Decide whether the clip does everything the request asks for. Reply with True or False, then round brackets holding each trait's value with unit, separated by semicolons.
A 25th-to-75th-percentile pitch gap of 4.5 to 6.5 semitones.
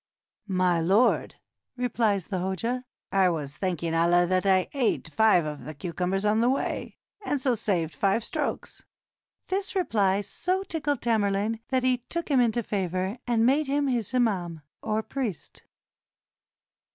True (5.3 semitones)